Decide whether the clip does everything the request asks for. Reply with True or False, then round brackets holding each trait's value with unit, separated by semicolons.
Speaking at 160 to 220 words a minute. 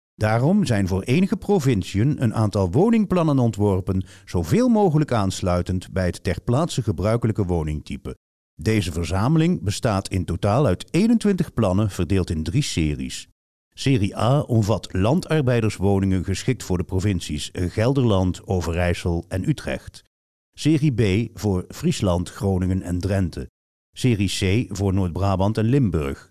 False (125 wpm)